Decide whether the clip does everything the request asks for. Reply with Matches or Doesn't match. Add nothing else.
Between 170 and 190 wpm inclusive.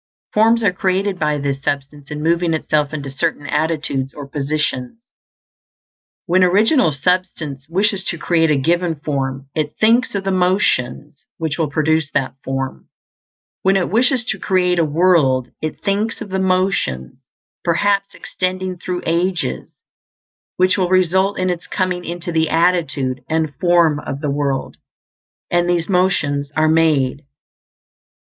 Doesn't match